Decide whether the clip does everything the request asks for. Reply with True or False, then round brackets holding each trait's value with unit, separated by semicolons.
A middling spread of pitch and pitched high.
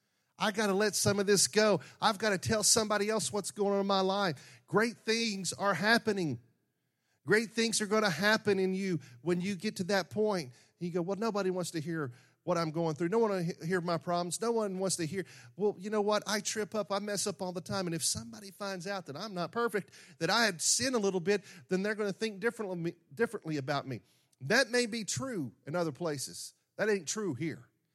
True (4.2 semitones; 195 Hz)